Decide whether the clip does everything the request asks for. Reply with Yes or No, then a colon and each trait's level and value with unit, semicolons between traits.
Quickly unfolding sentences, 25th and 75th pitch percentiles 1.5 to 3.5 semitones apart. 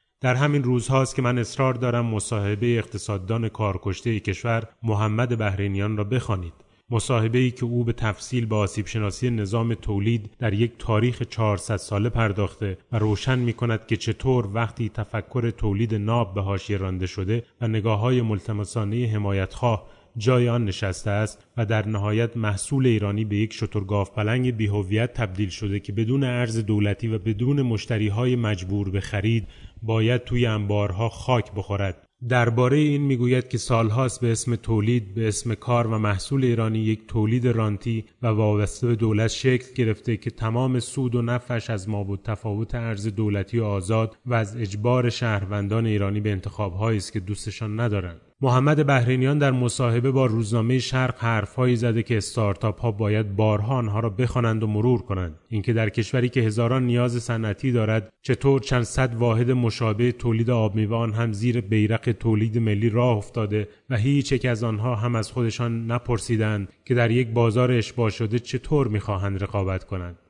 Yes: fast, 165 wpm; narrow, 2.5 semitones